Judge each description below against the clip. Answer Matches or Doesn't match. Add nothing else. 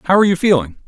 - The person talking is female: Doesn't match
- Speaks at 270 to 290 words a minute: Matches